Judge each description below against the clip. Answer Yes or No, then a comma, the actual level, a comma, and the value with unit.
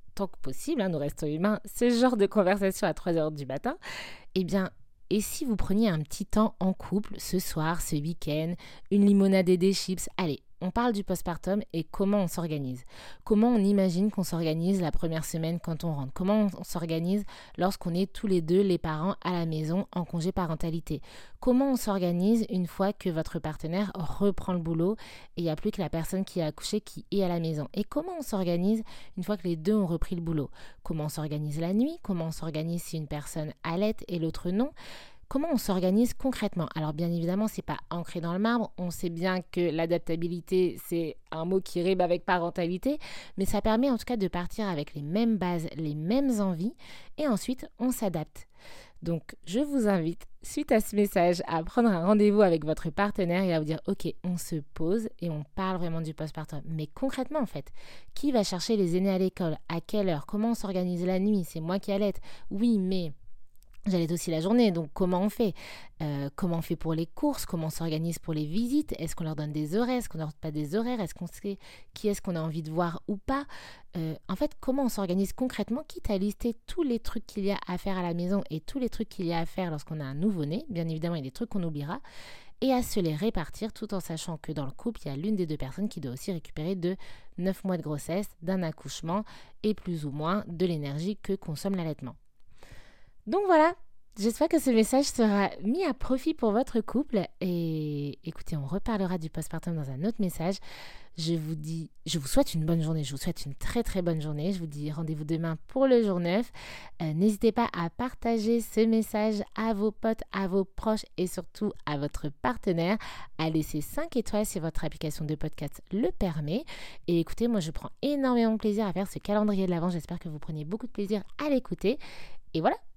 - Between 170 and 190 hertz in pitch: Yes, medium, 185 Hz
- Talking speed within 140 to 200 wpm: No, fast, 220 wpm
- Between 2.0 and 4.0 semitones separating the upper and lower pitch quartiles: No, average, 4.4 semitones